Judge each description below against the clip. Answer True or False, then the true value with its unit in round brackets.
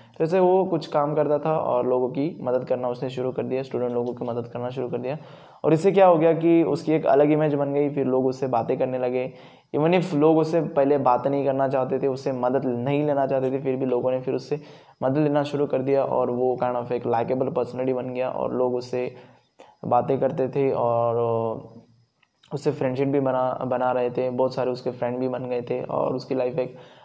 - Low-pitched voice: True (130 Hz)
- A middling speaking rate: False (230 wpm)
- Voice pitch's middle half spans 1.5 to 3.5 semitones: True (2.5 semitones)